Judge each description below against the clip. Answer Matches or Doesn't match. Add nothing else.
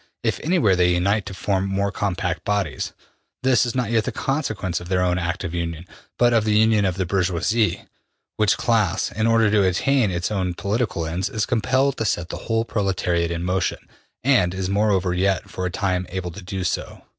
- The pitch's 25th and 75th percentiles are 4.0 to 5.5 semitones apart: Doesn't match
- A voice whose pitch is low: Matches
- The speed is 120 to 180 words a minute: Doesn't match